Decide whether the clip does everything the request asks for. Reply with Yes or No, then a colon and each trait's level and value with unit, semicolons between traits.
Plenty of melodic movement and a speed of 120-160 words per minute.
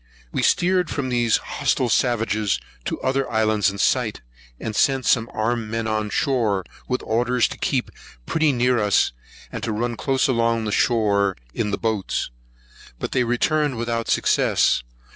No: average, 2.7 semitones; average, 155 wpm